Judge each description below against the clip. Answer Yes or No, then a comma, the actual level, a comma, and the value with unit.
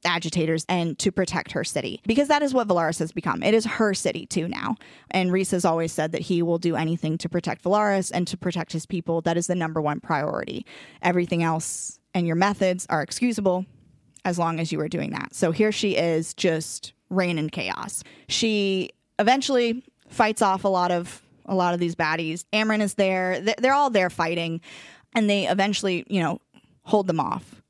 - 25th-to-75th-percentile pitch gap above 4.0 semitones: No, average, 3.2 semitones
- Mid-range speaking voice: Yes, medium, 180 Hz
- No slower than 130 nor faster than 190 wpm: No, average, 200 wpm